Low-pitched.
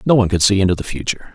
Yes: low, 100 Hz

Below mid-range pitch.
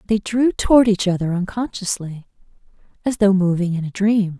No: high, 200 Hz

